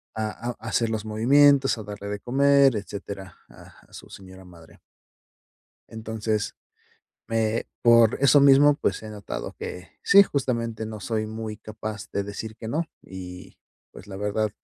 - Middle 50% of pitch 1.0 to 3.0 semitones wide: Yes, average, 2.7 semitones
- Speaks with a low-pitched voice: Yes, low, 110 Hz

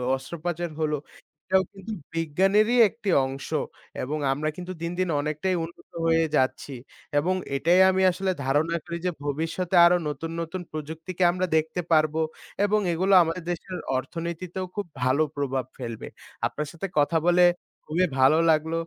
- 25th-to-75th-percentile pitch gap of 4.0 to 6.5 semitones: No, average, 3.3 semitones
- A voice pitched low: No, medium, 165 Hz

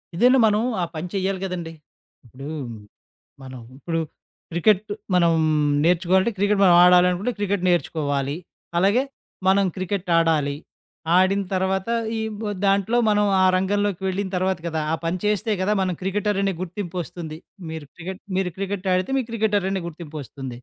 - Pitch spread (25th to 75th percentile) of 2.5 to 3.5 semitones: Yes, average, 3.0 semitones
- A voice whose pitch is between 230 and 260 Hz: No, medium, 185 Hz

